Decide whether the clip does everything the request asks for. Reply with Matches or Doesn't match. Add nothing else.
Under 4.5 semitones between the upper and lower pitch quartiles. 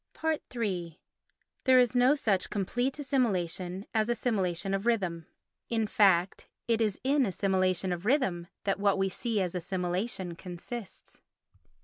Doesn't match